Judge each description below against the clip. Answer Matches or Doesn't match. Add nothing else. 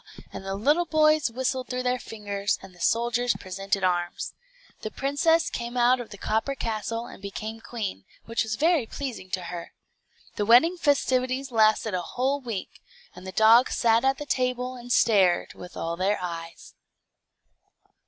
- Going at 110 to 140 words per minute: Doesn't match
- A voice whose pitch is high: Matches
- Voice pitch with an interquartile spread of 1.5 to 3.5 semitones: Doesn't match